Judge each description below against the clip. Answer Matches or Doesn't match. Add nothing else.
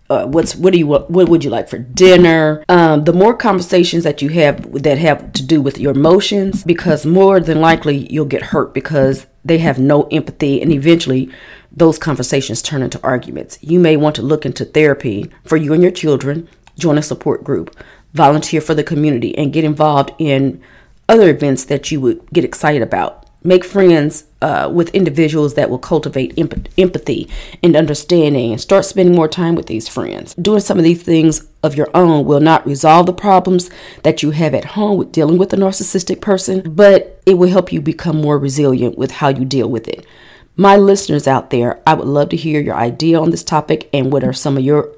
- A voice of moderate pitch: Matches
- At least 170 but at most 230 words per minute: Matches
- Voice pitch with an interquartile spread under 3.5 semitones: Doesn't match